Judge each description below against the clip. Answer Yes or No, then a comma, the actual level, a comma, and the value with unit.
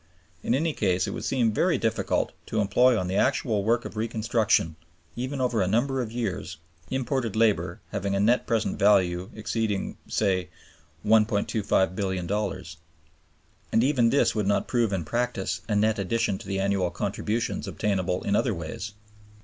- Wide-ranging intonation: No, average, 3.3 semitones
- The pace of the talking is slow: No, average, 155 wpm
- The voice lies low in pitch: Yes, low, 105 Hz